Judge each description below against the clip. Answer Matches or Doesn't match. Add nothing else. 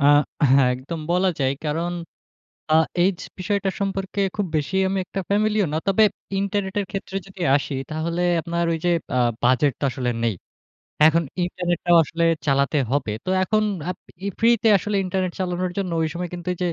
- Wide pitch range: Doesn't match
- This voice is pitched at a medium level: Matches